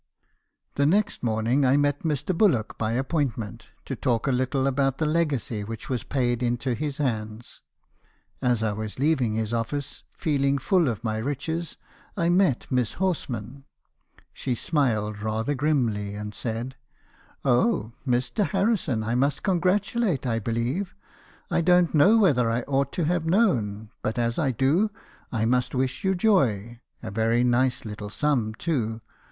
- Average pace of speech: Yes, average, 160 wpm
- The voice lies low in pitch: Yes, low, 130 Hz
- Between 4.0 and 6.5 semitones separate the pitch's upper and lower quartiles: Yes, average, 5.2 semitones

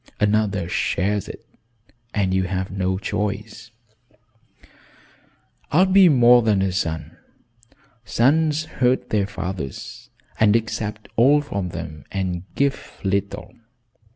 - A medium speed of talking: No, slow, 115 wpm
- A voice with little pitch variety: No, average, 4.4 semitones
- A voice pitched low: Yes, low, 105 Hz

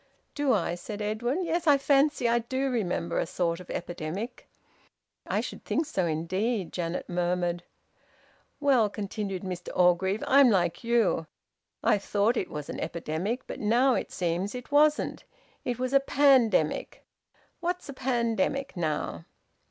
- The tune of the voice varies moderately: No, wide, 6.9 semitones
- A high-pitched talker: Yes, high, 215 Hz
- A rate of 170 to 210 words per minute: No, average, 145 wpm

